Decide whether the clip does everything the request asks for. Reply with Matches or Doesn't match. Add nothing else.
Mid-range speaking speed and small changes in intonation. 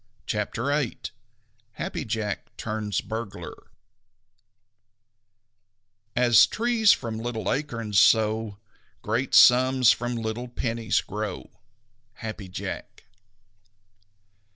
Doesn't match